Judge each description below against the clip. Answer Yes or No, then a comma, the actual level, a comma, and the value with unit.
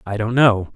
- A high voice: No, low, 110 Hz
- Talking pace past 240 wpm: No, fast, 235 wpm